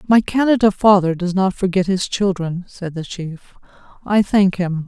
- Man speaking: No, female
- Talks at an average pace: Yes, average, 170 wpm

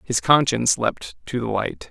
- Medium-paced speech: Yes, average, 190 wpm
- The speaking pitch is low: Yes, low, 120 Hz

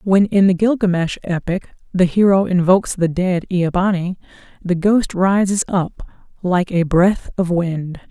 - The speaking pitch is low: No, medium, 185 Hz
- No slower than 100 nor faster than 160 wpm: Yes, average, 155 wpm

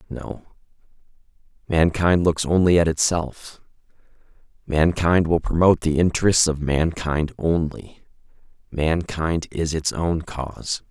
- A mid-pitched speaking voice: No, very low, 80 Hz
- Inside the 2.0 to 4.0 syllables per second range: Yes, 3.9 syllables/s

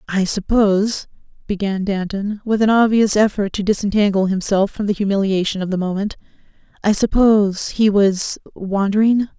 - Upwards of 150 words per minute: No, slow, 135 wpm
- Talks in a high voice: Yes, high, 205 Hz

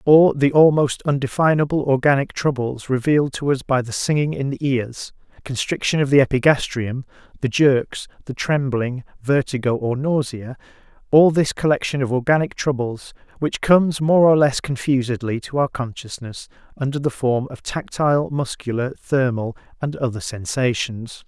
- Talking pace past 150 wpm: No, average, 140 wpm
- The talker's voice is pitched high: No, low, 135 Hz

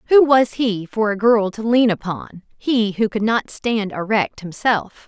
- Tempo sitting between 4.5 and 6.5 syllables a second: No, 4.1 syllables/s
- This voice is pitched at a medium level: No, high, 215 Hz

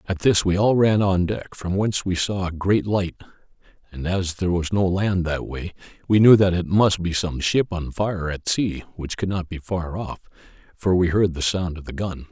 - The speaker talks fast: Yes, fast, 235 wpm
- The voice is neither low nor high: No, very low, 90 Hz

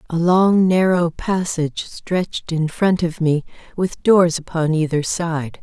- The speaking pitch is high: No, medium, 170 Hz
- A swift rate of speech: No, average, 150 wpm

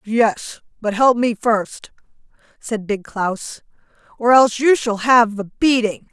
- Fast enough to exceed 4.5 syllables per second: No, 3.7 syllables/s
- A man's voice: No, female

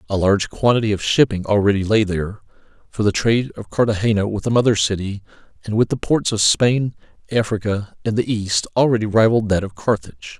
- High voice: No, low, 105 Hz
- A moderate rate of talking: Yes, average, 185 wpm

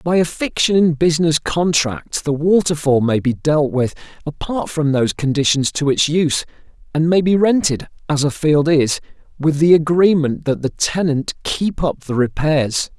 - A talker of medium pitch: Yes, medium, 155 Hz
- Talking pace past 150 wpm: Yes, average, 170 wpm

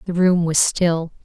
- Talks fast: No, average, 195 wpm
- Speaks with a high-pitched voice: No, medium, 170 Hz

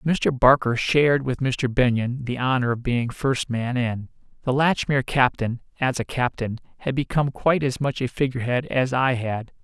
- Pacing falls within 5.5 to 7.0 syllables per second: No, 5.0 syllables/s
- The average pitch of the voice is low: Yes, low, 125 Hz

